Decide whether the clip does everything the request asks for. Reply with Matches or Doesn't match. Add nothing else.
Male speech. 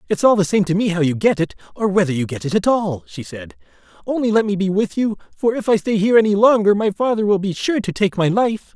Matches